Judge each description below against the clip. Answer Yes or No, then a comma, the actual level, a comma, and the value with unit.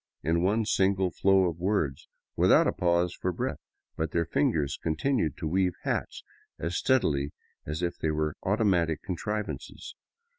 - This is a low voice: Yes, very low, 85 Hz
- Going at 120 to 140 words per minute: No, average, 150 wpm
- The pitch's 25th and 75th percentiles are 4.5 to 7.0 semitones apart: No, average, 3.5 semitones